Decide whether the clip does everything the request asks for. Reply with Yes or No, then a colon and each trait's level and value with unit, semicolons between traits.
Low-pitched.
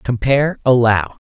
Yes: low, 125 Hz